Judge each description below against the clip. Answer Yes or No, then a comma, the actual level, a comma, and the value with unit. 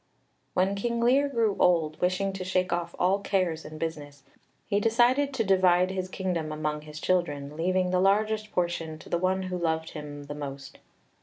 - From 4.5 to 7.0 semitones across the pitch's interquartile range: No, average, 3.8 semitones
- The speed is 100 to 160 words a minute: No, average, 180 wpm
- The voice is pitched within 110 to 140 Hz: No, medium, 180 Hz